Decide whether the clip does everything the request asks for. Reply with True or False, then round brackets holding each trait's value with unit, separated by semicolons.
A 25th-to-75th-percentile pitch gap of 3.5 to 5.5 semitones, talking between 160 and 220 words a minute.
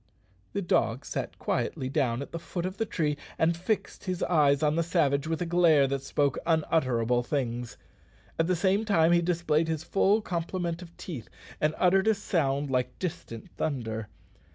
True (4.4 semitones; 180 wpm)